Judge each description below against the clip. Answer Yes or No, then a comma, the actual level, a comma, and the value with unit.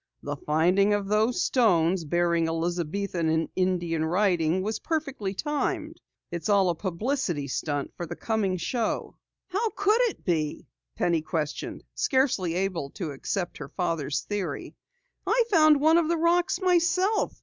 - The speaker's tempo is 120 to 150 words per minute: Yes, average, 145 wpm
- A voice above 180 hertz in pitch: Yes, high, 190 Hz